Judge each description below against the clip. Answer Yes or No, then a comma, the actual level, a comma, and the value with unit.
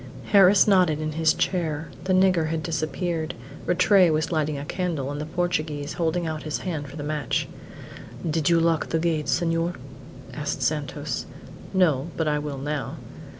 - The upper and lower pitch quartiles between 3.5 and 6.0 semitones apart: No, narrow, 2.6 semitones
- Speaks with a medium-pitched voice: Yes, medium, 160 Hz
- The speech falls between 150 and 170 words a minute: Yes, average, 165 wpm